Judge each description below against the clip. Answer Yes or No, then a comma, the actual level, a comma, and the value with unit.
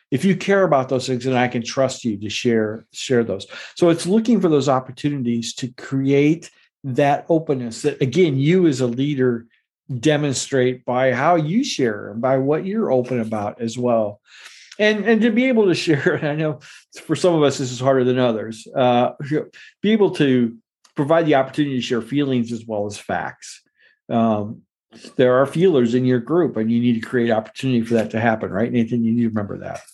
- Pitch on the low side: Yes, low, 130 Hz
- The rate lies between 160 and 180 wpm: No, average, 200 wpm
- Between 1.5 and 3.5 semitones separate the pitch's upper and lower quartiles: No, average, 4.4 semitones